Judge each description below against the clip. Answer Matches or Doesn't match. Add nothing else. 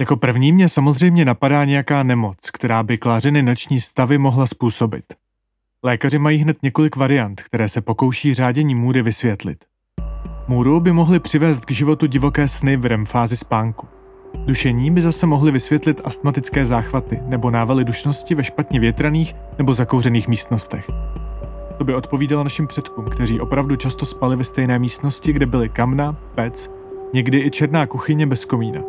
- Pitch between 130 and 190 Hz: Matches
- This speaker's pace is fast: Doesn't match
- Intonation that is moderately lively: Matches